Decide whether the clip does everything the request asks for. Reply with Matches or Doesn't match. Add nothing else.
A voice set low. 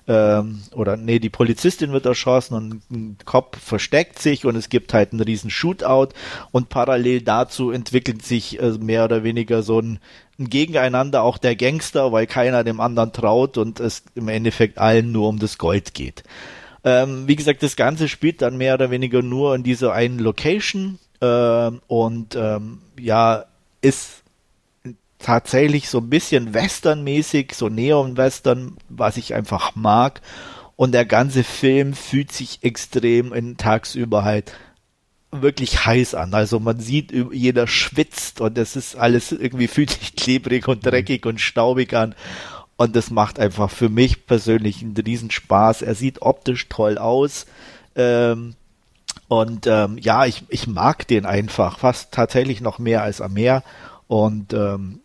Matches